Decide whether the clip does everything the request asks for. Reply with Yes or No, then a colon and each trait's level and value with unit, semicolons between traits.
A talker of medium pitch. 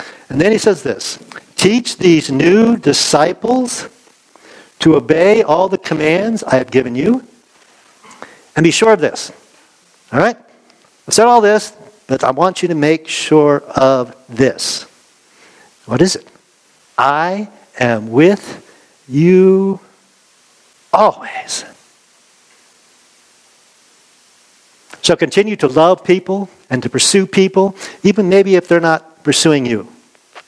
Yes: medium, 180 Hz